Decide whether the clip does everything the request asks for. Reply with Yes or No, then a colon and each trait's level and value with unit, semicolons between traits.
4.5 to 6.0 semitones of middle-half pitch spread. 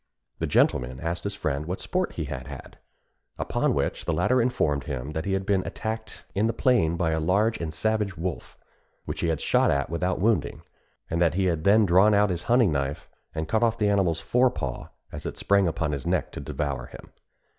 Yes: average, 5.2 semitones